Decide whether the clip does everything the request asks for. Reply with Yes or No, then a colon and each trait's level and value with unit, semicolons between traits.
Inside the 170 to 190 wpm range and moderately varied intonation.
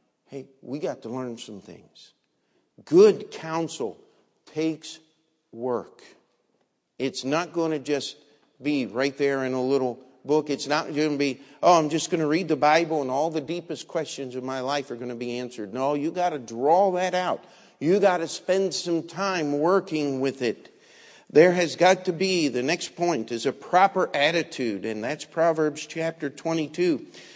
Yes: average, 180 wpm; average, 3.9 semitones